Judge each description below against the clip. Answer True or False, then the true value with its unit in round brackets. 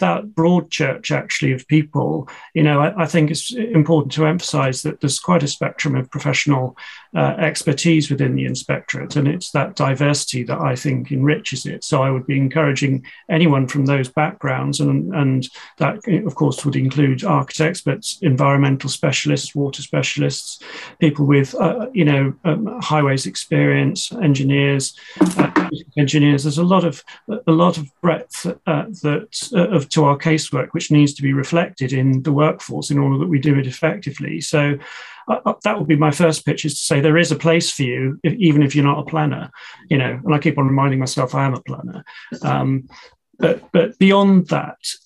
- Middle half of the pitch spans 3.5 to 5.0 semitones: False (2.7 semitones)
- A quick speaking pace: False (190 wpm)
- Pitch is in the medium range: True (150 Hz)